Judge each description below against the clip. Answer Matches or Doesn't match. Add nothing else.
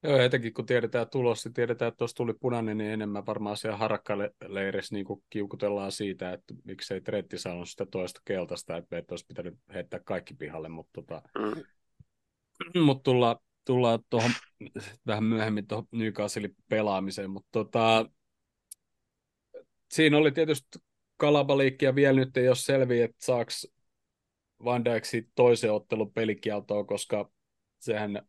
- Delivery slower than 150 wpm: Matches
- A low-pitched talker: Matches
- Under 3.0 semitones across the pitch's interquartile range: Doesn't match